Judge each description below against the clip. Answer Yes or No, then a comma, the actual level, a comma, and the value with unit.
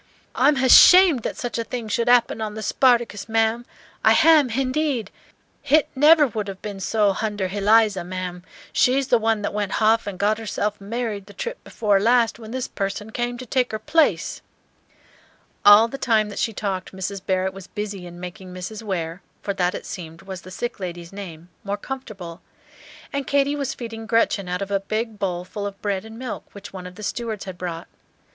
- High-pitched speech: Yes, high, 215 Hz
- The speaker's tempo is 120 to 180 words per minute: No, average, 195 wpm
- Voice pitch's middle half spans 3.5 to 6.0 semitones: Yes, average, 3.8 semitones